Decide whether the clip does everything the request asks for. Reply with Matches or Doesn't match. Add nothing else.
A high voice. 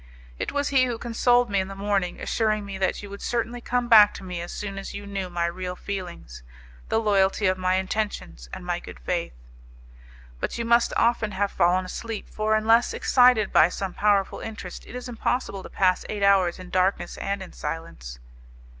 Matches